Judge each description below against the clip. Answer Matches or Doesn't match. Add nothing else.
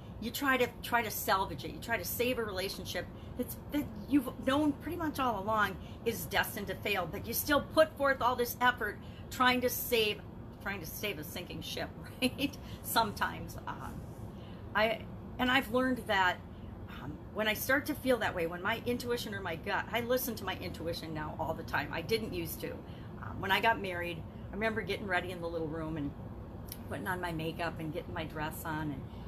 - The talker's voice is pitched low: Doesn't match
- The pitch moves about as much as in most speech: Doesn't match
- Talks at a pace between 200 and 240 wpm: Matches